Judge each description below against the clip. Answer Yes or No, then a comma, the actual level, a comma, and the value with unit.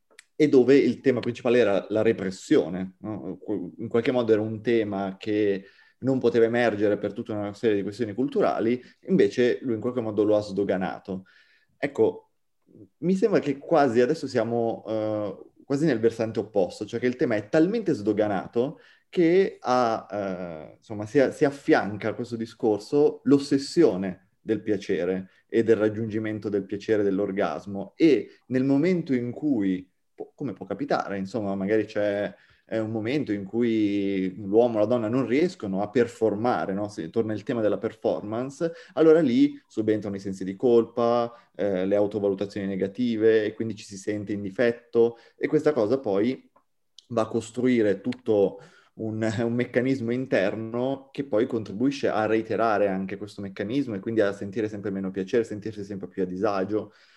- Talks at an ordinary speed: Yes, average, 160 wpm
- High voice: No, low, 110 Hz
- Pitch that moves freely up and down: No, average, 3.3 semitones